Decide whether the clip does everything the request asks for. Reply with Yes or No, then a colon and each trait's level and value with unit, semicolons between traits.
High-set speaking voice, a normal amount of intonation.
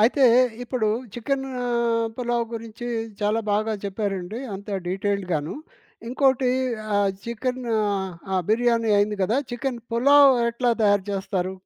Yes: high, 220 Hz; average, 3.3 semitones